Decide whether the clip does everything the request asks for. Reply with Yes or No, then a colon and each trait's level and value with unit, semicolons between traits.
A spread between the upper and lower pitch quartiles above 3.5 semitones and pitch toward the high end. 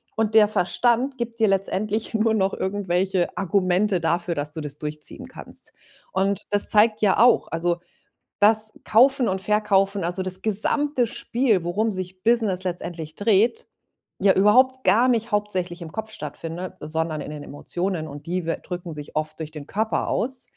Yes: average, 4.1 semitones; high, 195 Hz